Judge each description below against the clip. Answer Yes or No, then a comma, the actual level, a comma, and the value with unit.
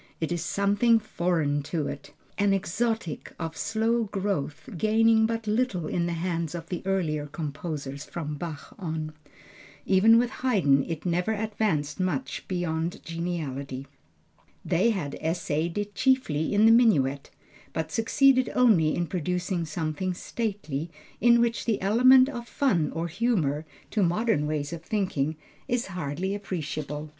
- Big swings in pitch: Yes, wide, 5.9 semitones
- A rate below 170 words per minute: Yes, average, 140 wpm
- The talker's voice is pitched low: No, medium, 175 Hz